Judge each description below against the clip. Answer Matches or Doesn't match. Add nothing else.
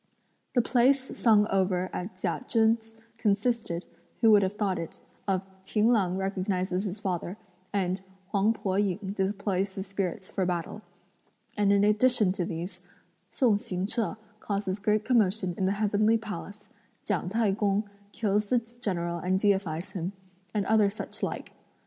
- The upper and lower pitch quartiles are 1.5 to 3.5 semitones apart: Matches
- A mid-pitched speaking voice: Doesn't match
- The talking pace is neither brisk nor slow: Matches